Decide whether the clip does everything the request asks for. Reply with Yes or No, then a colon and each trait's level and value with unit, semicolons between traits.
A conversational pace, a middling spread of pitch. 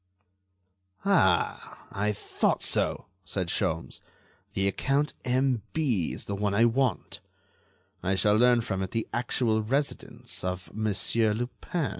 No: slow, 125 wpm; average, 4.2 semitones